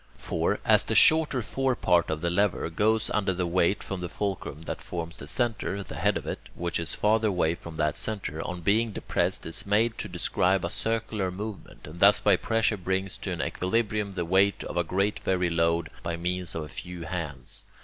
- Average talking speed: No, fast, 210 wpm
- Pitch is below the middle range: Yes, very low, 95 Hz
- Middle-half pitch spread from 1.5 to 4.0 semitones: Yes, average, 3.7 semitones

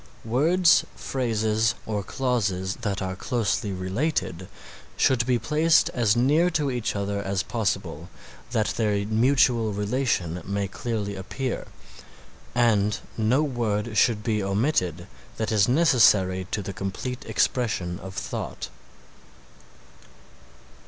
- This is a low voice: Yes, low, 110 Hz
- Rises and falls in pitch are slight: No, average, 4.1 semitones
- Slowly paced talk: Yes, slow, 115 wpm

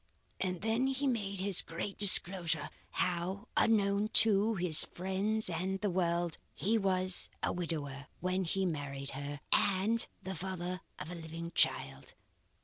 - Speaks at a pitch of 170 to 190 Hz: Yes, medium, 185 Hz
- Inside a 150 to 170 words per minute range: No, average, 140 wpm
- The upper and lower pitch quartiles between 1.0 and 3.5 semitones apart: Yes, average, 3.1 semitones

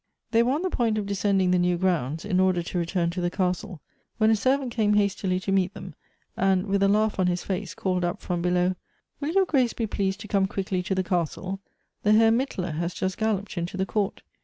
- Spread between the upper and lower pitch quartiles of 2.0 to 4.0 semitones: Yes, average, 2.9 semitones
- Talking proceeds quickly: Yes, fast, 235 wpm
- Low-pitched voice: No, high, 190 Hz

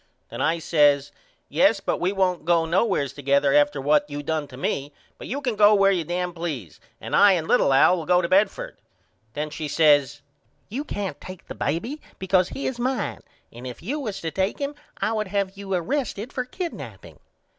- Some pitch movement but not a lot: No, wide, 5.7 semitones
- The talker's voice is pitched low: No, medium, 180 Hz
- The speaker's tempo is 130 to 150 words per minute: No, average, 200 wpm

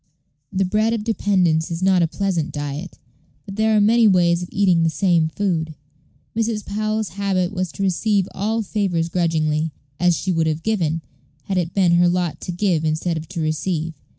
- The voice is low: No, medium, 180 Hz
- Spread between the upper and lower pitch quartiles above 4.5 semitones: No, average, 3.5 semitones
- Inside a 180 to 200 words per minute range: Yes, average, 185 wpm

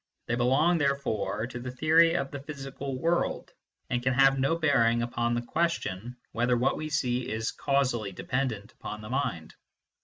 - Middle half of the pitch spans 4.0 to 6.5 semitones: No, average, 3.0 semitones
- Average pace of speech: Yes, average, 165 wpm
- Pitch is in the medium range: No, low, 130 Hz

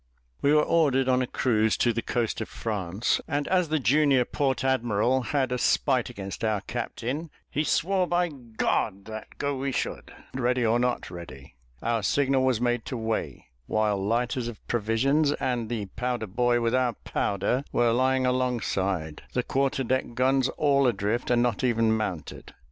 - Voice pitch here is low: Yes, low, 125 Hz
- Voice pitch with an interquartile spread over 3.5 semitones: No, average, 3.0 semitones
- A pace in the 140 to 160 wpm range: No, average, 170 wpm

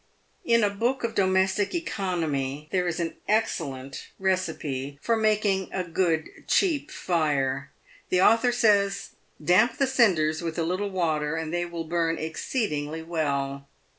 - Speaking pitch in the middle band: Yes, medium, 175 Hz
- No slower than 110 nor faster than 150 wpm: Yes, average, 145 wpm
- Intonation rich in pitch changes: No, average, 4.8 semitones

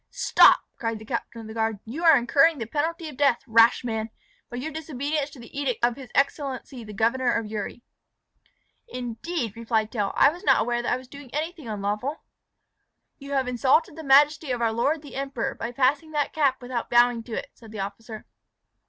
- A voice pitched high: Yes, very high, 250 Hz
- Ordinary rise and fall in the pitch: Yes, average, 3.9 semitones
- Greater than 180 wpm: Yes, average, 200 wpm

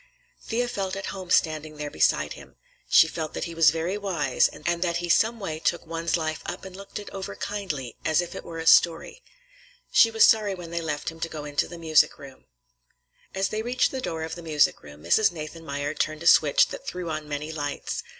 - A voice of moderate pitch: Yes, medium, 165 Hz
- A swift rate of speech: Yes, fast, 220 wpm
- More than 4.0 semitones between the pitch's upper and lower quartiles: No, average, 3.7 semitones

